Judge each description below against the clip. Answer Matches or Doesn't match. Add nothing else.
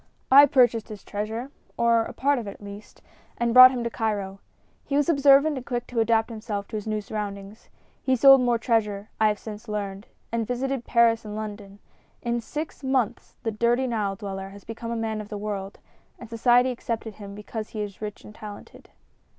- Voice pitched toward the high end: Matches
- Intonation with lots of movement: Doesn't match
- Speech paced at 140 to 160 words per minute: Doesn't match